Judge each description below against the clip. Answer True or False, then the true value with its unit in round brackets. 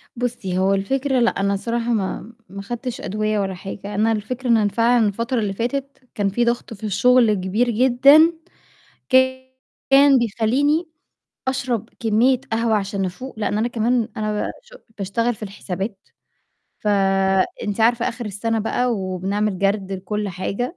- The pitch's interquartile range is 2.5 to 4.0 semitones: True (3.6 semitones)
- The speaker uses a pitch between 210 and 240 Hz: True (225 Hz)